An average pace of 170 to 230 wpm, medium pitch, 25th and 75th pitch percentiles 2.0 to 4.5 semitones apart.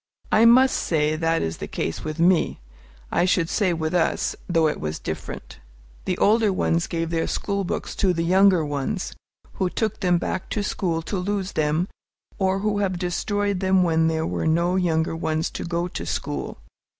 Yes: average, 185 wpm; medium, 175 Hz; average, 2.9 semitones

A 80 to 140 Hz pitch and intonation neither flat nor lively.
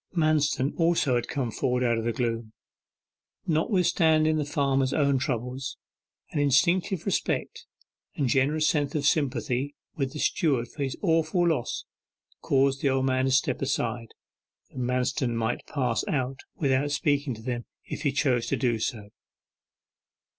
Yes: low, 135 Hz; average, 3.3 semitones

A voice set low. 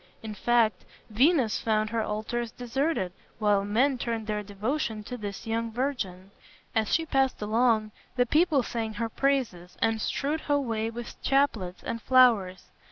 No: high, 230 Hz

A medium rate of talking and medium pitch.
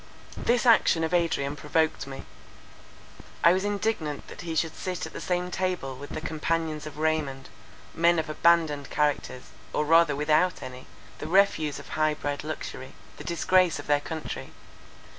Yes: average, 160 wpm; medium, 160 Hz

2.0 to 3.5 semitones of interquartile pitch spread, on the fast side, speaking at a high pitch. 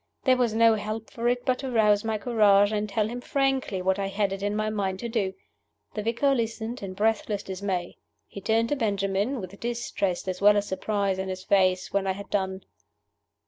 Yes: average, 2.8 semitones; fast, 210 wpm; high, 210 Hz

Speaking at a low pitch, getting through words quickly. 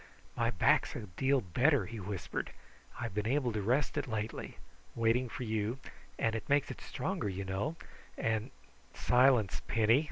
No: low, 115 Hz; average, 165 wpm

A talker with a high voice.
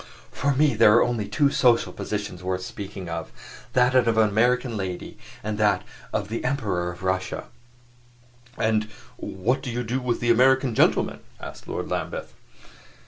No: low, 110 Hz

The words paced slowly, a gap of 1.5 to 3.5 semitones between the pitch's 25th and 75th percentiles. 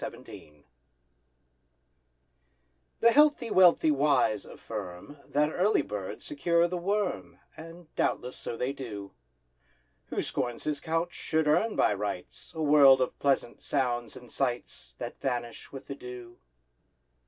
No: slow, 130 wpm; wide, 5.6 semitones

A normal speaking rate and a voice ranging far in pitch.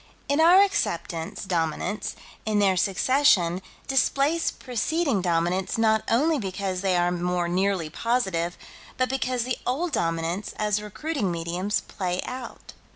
No: slow, 130 wpm; wide, 6.4 semitones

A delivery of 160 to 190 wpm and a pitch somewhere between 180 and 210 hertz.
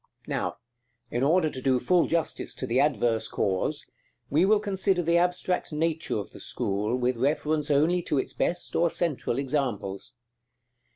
No: average, 170 wpm; medium, 150 Hz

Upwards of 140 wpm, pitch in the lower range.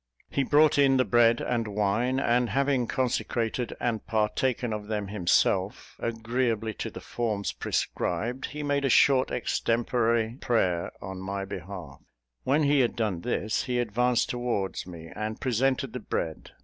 Yes: average, 150 wpm; low, 115 Hz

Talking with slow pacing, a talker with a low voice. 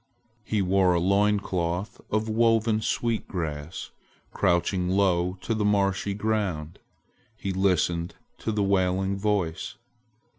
Yes: slow, 120 wpm; very low, 95 Hz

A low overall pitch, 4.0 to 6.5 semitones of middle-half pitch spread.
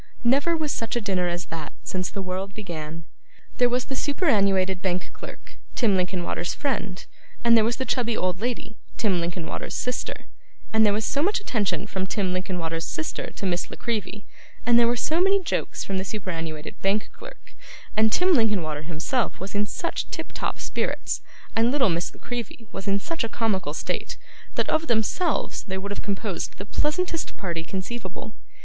No: high, 205 Hz; average, 4.7 semitones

